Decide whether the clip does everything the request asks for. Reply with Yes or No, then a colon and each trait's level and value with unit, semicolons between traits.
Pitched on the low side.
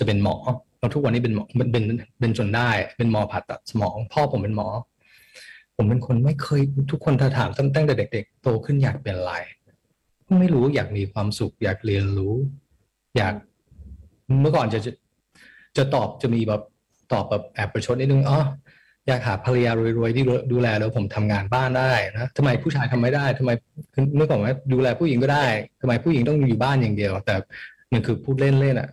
Yes: low, 125 Hz